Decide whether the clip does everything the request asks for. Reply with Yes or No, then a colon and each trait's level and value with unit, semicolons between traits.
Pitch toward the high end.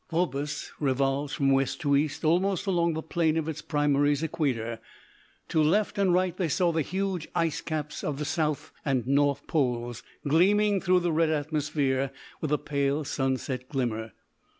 No: medium, 150 Hz